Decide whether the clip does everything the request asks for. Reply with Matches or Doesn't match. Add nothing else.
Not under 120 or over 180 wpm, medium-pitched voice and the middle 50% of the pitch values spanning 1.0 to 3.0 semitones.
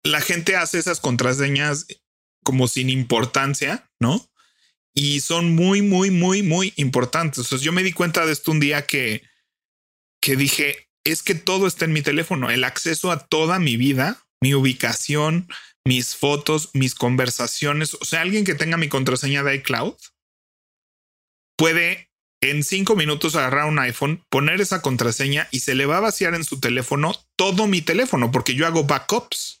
Doesn't match